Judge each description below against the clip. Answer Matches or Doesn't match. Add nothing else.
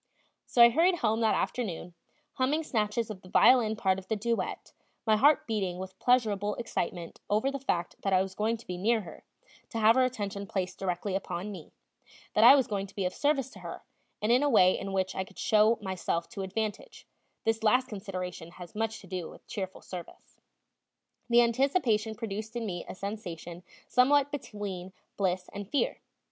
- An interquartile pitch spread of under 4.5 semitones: Matches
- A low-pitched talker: Doesn't match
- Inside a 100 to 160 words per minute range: Doesn't match